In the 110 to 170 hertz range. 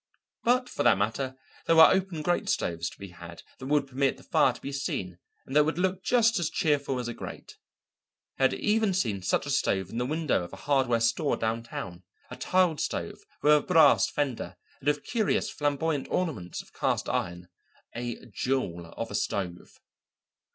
Yes: low, 135 Hz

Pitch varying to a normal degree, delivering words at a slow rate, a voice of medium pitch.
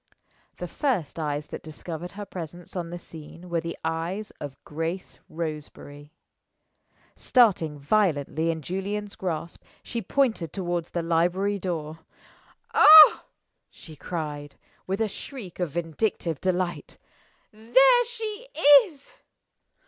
Yes: average, 4.4 semitones; slow, 120 wpm; medium, 175 Hz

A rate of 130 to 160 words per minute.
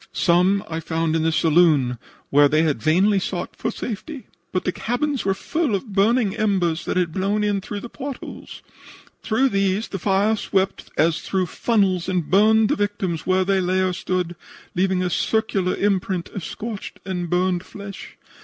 No: average, 180 wpm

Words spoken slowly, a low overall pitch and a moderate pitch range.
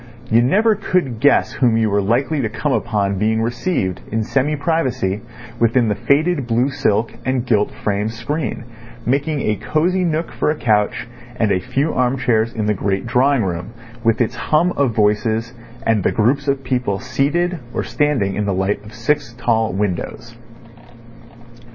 No: average, 170 wpm; low, 120 Hz; average, 4.7 semitones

